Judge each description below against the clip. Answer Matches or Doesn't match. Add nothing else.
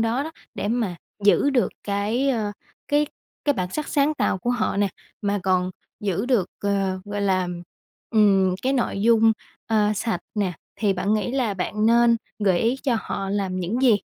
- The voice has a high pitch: Matches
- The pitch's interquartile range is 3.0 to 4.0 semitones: Matches